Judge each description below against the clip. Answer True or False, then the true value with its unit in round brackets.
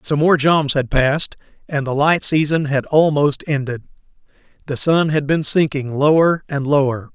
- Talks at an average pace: True (170 wpm)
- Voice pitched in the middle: True (145 Hz)